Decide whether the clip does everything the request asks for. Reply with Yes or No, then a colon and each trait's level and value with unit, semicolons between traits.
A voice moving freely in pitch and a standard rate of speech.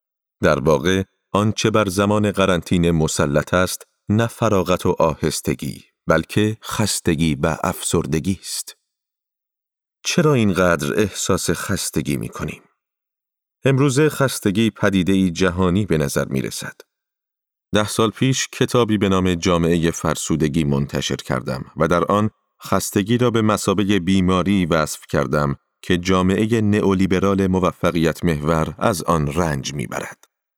No: average, 4.0 semitones; average, 120 wpm